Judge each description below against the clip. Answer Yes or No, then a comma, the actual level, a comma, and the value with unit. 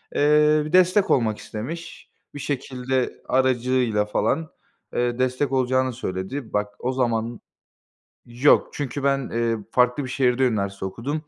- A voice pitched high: No, low, 130 Hz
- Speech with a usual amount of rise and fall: Yes, average, 3.1 semitones